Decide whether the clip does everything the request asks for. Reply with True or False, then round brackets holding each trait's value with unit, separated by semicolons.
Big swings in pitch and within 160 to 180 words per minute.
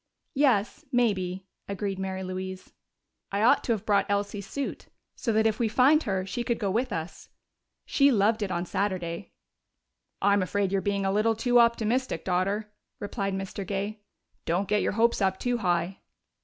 False (3.0 semitones; 170 wpm)